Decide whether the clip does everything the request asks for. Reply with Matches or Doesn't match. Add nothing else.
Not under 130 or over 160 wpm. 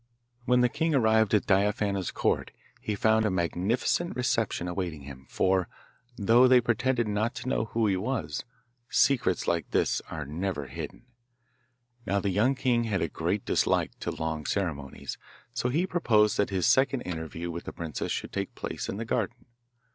Doesn't match